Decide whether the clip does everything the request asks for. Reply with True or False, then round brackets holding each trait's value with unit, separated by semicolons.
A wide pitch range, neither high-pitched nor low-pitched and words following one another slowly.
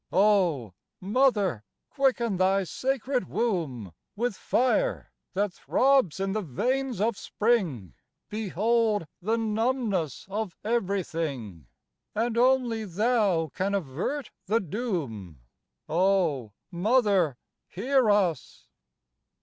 False (6.0 semitones; 200 Hz; 95 wpm)